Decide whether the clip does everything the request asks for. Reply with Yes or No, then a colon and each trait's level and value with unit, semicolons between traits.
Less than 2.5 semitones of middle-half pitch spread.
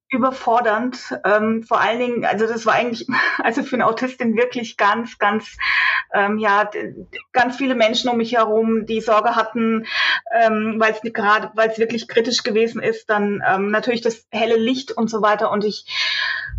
Yes: narrow, 1.6 semitones